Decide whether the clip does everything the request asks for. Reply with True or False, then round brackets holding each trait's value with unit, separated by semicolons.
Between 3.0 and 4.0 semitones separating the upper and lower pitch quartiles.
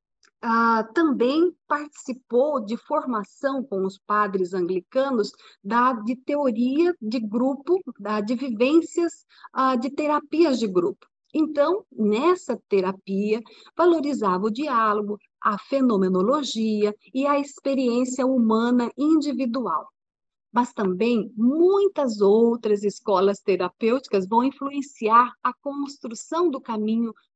False (4.8 semitones)